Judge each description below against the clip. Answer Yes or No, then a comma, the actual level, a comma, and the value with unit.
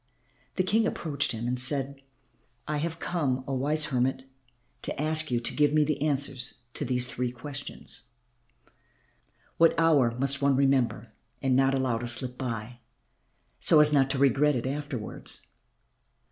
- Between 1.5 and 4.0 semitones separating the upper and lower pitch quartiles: Yes, average, 2.9 semitones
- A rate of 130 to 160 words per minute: Yes, average, 155 wpm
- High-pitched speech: No, low, 135 Hz